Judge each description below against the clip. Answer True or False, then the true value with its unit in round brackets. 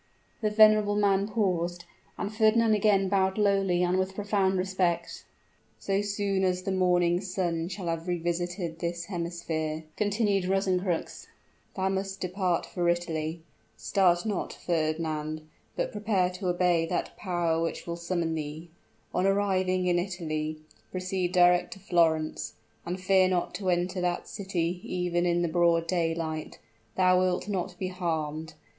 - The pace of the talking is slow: False (145 wpm)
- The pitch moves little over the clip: True (2.2 semitones)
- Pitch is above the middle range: False (180 Hz)